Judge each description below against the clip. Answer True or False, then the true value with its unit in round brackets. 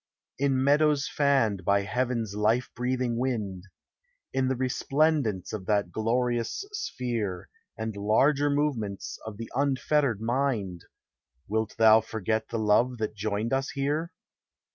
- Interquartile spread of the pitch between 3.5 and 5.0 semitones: True (4.2 semitones)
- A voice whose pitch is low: True (115 Hz)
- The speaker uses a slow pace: True (125 wpm)